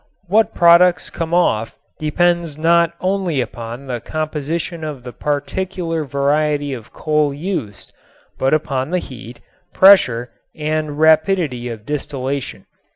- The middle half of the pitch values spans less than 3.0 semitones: No, average, 4.1 semitones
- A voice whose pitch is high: No, medium, 150 Hz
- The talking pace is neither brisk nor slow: No, slow, 120 wpm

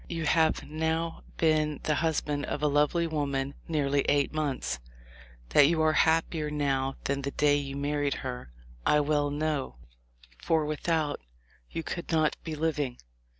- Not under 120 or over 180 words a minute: Yes, average, 150 wpm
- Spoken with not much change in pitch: Yes, narrow, 2.0 semitones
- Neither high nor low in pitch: Yes, medium, 150 Hz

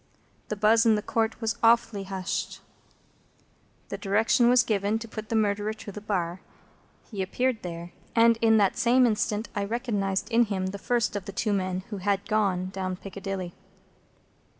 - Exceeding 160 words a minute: Yes, average, 175 wpm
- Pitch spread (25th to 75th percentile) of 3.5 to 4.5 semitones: No, narrow, 2.6 semitones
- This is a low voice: No, high, 210 Hz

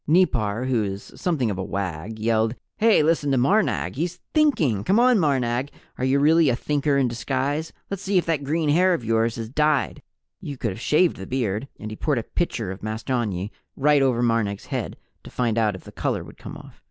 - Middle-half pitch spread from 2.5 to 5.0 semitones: No, wide, 5.6 semitones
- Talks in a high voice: No, low, 130 Hz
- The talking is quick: Yes, fast, 215 wpm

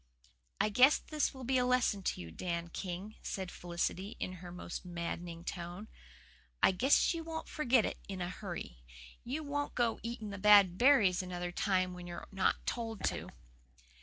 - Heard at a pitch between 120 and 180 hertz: No, high, 195 Hz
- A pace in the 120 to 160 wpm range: No, average, 175 wpm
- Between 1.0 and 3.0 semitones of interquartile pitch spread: No, wide, 5.5 semitones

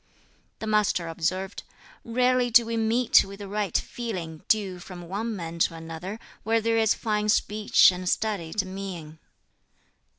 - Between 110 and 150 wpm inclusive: Yes, average, 145 wpm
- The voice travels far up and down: No, average, 4.0 semitones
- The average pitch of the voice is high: Yes, high, 200 Hz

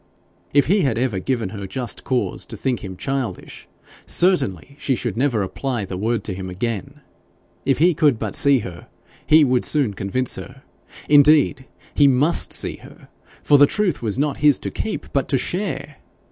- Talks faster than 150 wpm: Yes, average, 180 wpm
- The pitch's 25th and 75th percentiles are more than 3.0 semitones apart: Yes, average, 4.6 semitones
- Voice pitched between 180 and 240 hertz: No, low, 130 Hz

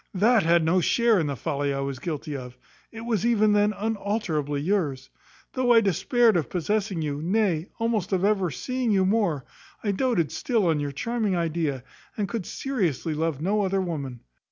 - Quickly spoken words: No, average, 180 wpm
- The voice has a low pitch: No, medium, 185 Hz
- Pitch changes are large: Yes, wide, 6.0 semitones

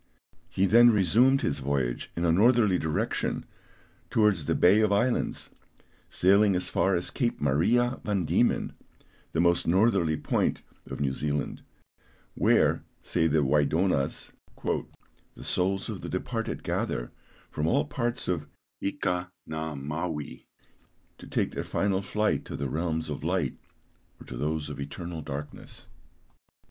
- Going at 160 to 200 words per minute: No, average, 140 wpm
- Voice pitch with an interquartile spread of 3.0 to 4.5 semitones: No, average, 5.2 semitones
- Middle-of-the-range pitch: No, very low, 85 Hz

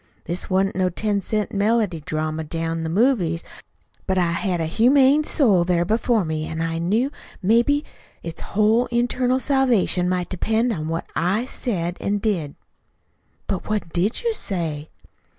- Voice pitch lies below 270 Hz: Yes, high, 190 Hz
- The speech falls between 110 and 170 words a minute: Yes, average, 155 wpm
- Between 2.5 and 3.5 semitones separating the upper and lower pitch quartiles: No, wide, 5.6 semitones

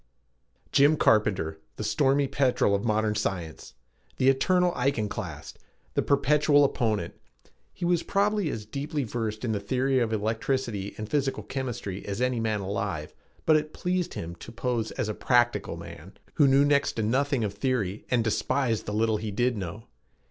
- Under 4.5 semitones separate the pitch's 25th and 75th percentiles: No, average, 4.8 semitones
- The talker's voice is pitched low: Yes, low, 120 Hz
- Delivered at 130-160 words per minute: No, average, 170 wpm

